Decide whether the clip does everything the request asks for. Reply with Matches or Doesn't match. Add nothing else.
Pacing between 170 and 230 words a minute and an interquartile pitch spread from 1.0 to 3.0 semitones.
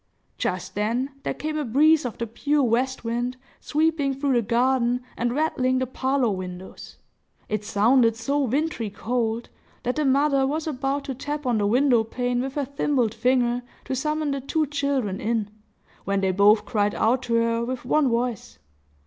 Doesn't match